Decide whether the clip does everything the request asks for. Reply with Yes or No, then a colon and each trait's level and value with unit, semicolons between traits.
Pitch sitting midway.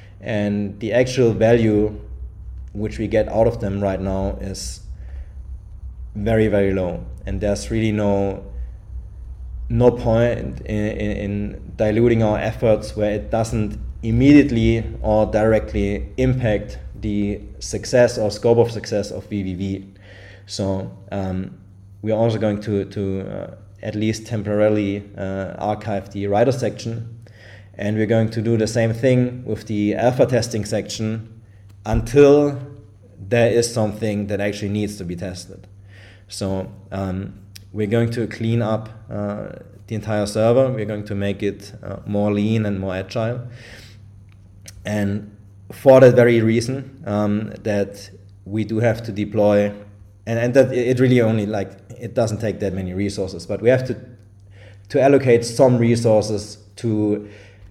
No: low, 105 Hz